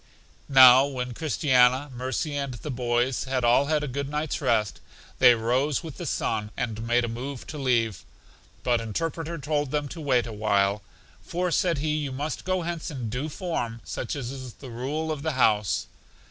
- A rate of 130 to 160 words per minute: No, average, 185 wpm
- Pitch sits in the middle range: No, low, 130 Hz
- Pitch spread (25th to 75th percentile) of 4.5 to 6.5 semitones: No, average, 3.9 semitones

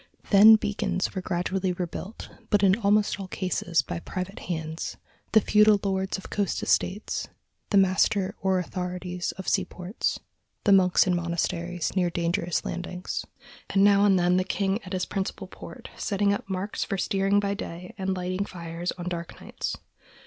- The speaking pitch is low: No, medium, 185 Hz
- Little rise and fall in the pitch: Yes, narrow, 1.9 semitones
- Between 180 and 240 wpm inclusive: No, average, 165 wpm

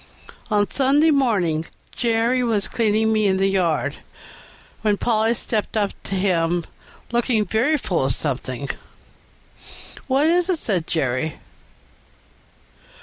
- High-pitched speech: Yes, high, 210 Hz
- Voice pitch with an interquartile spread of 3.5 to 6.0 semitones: Yes, wide, 5.6 semitones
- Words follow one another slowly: Yes, slow, 120 wpm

